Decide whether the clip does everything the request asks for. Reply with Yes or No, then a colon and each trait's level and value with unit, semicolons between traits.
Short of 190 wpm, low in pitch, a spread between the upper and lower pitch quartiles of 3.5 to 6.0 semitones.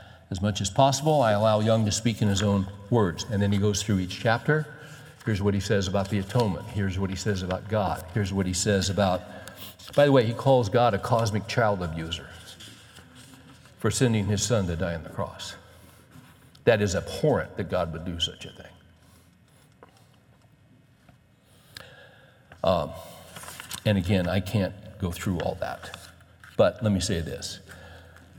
Yes: average, 170 wpm; low, 100 Hz; average, 3.8 semitones